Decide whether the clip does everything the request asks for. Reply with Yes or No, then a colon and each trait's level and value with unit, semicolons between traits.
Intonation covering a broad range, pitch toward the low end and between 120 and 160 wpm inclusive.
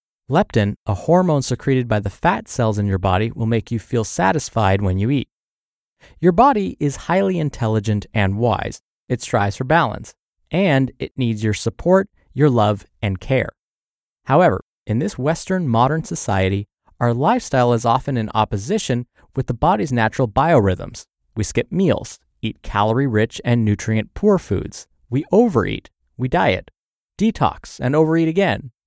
Yes: wide, 6.0 semitones; low, 120 Hz; average, 155 wpm